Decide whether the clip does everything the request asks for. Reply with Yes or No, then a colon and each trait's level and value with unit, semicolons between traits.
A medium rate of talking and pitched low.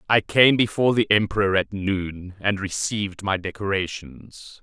Yes: average, 145 wpm; low, 100 Hz